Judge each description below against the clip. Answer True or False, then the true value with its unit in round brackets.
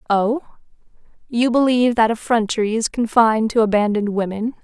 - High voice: True (225 Hz)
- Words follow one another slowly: True (130 wpm)